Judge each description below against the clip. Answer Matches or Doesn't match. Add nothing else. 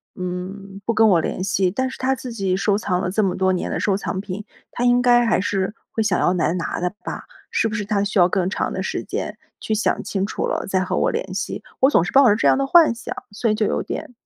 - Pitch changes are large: Doesn't match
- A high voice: Matches